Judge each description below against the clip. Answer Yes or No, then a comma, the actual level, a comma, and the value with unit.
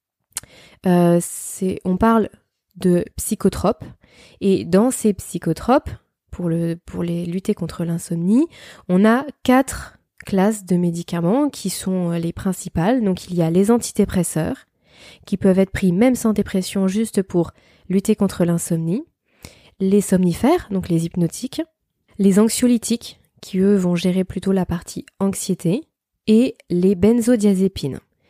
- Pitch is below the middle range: No, high, 190 Hz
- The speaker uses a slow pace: Yes, slow, 135 wpm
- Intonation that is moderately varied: Yes, average, 3.8 semitones